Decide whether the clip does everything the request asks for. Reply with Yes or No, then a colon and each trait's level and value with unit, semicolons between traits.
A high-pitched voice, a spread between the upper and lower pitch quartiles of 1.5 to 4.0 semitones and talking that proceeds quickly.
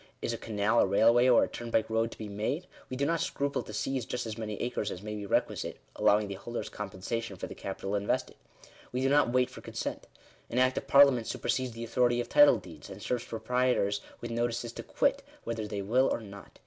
No: low, 115 Hz; average, 3.2 semitones; fast, 225 wpm